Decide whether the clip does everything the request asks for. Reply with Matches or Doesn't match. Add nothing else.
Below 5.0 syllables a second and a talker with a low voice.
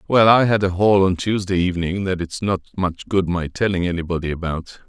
Doesn't match